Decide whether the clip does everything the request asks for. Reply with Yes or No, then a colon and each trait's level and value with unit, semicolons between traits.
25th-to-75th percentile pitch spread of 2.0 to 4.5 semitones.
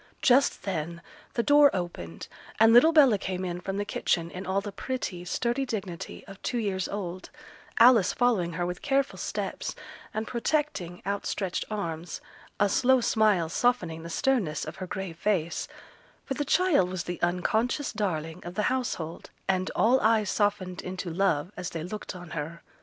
No: average, 5.1 semitones